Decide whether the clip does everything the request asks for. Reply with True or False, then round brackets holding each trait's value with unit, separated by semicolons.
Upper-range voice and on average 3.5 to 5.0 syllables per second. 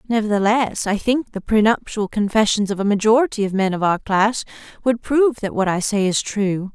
False (215 Hz; 5.3 syllables/s)